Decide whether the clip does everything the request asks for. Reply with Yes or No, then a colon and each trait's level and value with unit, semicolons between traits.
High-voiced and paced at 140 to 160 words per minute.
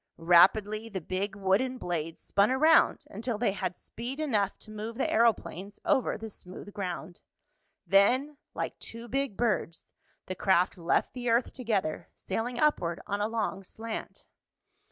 Yes: high, 210 Hz; average, 150 wpm